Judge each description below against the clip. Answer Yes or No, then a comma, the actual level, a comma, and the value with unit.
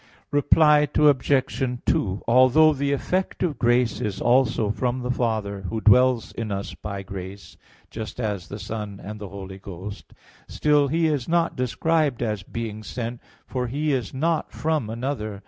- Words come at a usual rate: Yes, average, 160 wpm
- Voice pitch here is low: Yes, low, 120 Hz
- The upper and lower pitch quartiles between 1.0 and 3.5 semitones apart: No, average, 5.2 semitones